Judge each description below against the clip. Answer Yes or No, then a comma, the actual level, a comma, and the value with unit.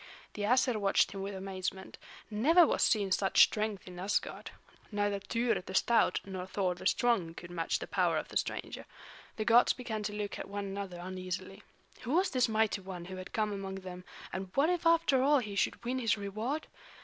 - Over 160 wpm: Yes, average, 200 wpm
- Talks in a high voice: Yes, high, 205 Hz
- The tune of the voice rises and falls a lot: No, average, 3.8 semitones